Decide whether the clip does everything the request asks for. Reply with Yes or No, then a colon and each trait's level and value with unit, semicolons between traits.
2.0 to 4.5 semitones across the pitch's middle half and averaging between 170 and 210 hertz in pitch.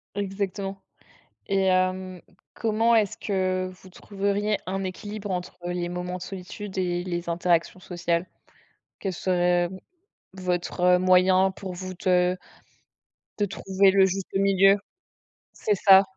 No: narrow, 1.5 semitones; medium, 185 Hz